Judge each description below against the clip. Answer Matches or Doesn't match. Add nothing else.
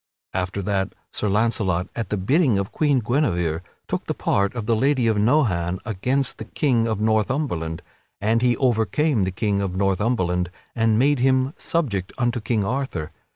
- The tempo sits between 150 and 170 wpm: Matches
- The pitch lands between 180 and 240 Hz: Doesn't match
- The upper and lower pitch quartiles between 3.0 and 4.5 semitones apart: Doesn't match